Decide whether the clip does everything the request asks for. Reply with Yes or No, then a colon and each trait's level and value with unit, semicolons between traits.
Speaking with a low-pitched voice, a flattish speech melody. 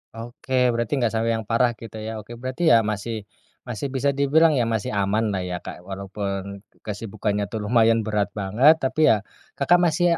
No: low, 115 Hz; average, 3.6 semitones